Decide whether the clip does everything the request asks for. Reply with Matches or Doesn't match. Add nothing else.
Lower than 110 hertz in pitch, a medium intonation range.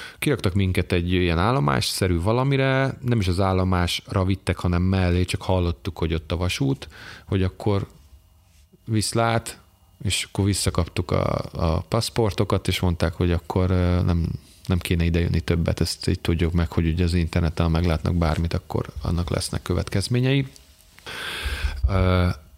Matches